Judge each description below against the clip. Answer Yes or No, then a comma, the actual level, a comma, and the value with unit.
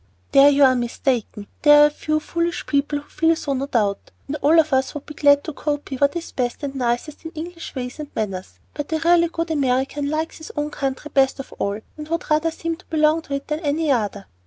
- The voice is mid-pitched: No, very high, 290 Hz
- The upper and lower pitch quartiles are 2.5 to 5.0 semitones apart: Yes, average, 2.9 semitones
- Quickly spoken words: Yes, fast, 235 wpm